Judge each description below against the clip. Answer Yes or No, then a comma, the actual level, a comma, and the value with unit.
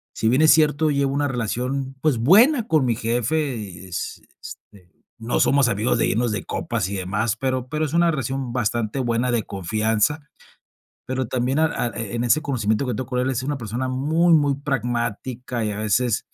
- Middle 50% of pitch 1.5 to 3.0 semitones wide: No, average, 3.8 semitones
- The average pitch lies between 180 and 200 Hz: No, low, 125 Hz